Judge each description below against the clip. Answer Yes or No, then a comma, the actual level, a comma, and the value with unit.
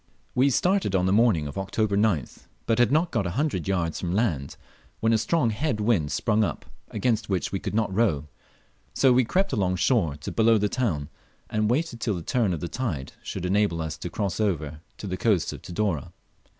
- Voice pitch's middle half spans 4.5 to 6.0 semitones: Yes, average, 5.1 semitones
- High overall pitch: No, low, 105 Hz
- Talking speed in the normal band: No, fast, 210 wpm